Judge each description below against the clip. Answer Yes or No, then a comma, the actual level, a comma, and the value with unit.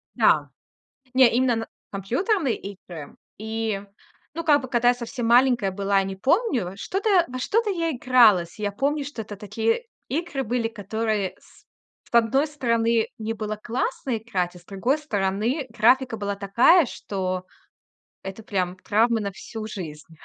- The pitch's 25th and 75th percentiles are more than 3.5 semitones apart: Yes, average, 4.7 semitones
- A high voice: Yes, high, 225 Hz